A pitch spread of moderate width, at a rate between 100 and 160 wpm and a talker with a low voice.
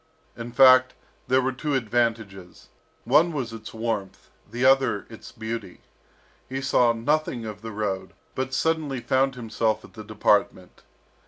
Yes: average, 3.3 semitones; average, 145 wpm; low, 120 Hz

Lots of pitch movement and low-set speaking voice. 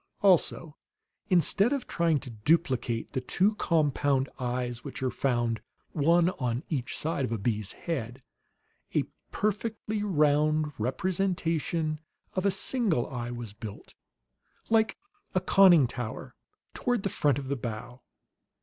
No: wide, 6.8 semitones; medium, 150 Hz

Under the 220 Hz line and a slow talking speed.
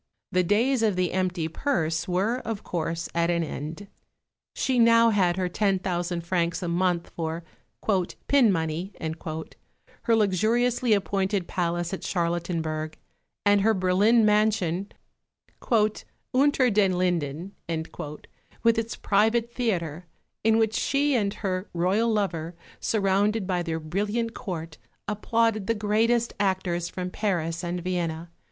Yes: high, 190 Hz; slow, 130 wpm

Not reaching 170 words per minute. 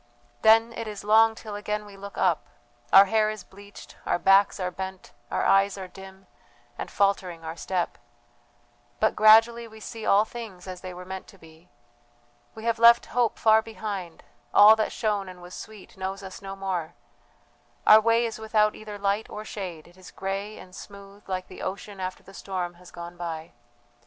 No: average, 185 wpm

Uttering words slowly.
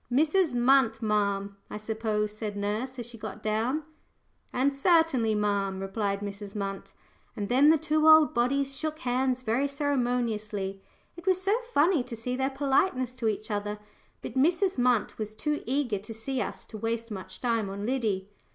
No: average, 170 wpm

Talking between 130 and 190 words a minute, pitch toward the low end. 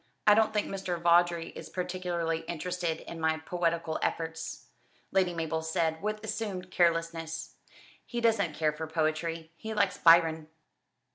No: average, 140 wpm; medium, 170 Hz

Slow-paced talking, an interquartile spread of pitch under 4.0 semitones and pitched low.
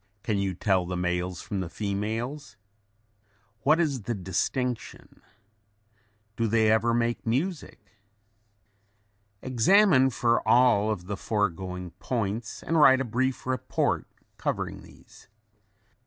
No: slow, 110 wpm; average, 4.6 semitones; low, 115 Hz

